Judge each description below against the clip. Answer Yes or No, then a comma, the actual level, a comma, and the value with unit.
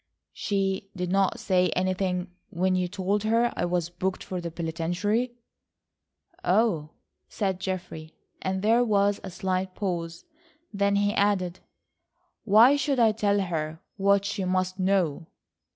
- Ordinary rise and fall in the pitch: No, narrow, 2.2 semitones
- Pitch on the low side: No, high, 190 Hz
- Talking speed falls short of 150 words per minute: Yes, slow, 135 wpm